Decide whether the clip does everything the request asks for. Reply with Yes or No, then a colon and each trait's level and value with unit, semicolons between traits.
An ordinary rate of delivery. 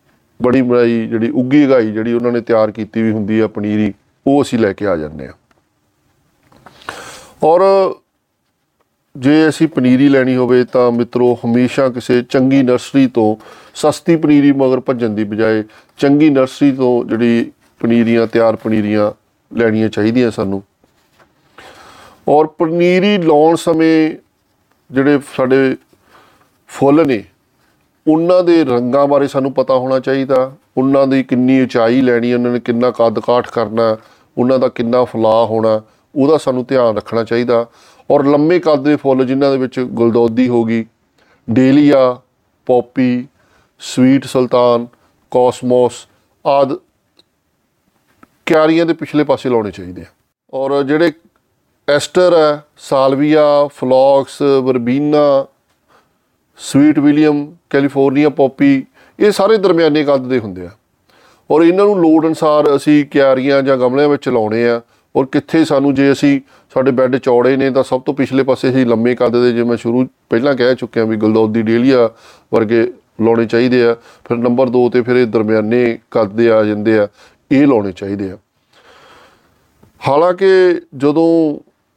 Yes: average, 140 wpm